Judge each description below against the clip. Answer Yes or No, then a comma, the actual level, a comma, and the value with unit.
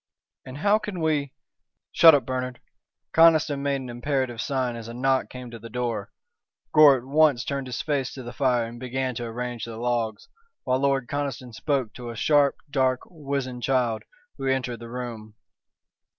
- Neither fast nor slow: Yes, average, 180 wpm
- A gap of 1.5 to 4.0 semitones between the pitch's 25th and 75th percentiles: Yes, narrow, 2.6 semitones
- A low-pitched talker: Yes, low, 130 Hz